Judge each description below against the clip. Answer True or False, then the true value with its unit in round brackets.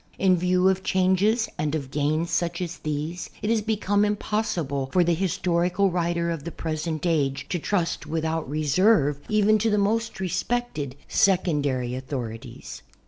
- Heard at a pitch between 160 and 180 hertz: True (170 Hz)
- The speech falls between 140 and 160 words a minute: True (155 wpm)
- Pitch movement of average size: True (4.5 semitones)